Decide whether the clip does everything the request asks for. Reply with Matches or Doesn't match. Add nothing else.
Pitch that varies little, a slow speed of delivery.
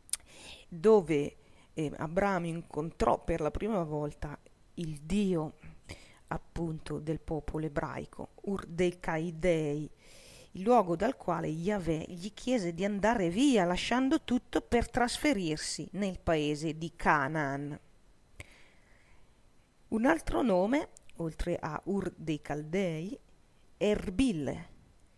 Doesn't match